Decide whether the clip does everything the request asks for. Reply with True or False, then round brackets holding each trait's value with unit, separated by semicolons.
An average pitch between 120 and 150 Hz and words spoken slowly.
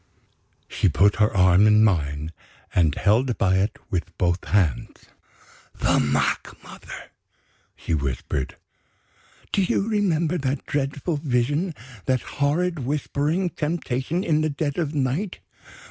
True (135 Hz; 125 wpm)